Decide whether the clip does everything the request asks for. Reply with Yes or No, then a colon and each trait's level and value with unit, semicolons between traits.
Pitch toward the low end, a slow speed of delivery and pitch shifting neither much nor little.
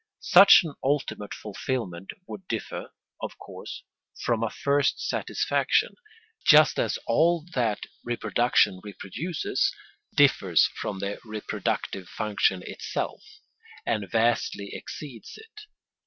No: low, 115 Hz; slow, 105 wpm; wide, 6.3 semitones